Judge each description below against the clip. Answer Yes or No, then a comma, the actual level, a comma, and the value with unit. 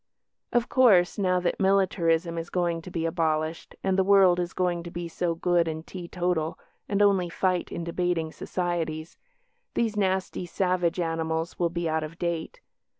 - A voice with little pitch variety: Yes, narrow, 1.9 semitones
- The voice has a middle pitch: Yes, medium, 175 Hz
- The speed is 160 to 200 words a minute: Yes, average, 165 wpm